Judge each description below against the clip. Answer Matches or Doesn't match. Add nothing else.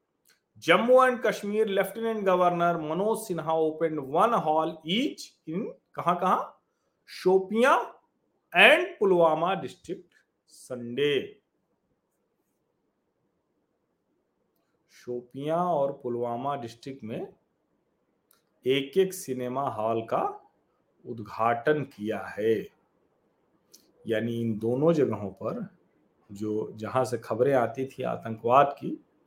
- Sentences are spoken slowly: Matches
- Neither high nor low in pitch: Matches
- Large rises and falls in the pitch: Matches